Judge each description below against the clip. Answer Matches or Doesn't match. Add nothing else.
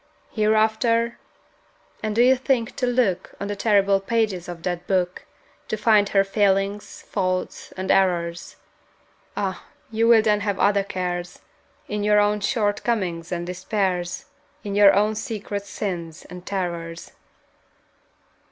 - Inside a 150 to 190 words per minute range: Doesn't match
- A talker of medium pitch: Doesn't match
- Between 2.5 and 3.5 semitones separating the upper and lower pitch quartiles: Matches